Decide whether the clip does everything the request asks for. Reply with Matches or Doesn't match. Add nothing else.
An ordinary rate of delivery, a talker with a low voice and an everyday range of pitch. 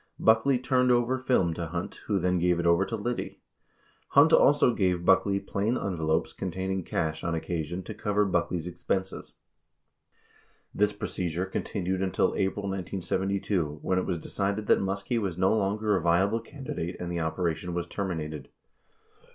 Matches